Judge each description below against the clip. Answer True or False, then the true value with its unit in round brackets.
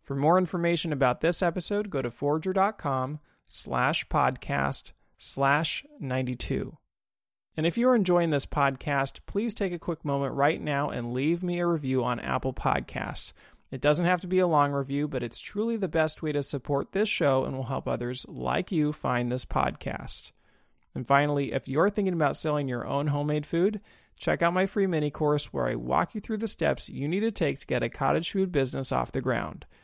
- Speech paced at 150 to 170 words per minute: False (195 wpm)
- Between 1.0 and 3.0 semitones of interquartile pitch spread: False (4.6 semitones)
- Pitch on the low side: False (150 Hz)